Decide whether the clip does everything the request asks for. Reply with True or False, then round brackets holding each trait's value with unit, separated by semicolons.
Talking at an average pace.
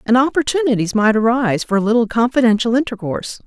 True (155 wpm)